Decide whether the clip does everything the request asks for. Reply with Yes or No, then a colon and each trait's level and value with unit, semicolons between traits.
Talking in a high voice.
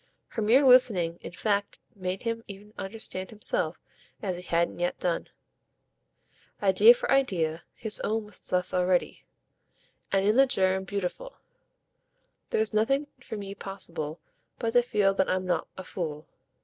Yes: high, 195 Hz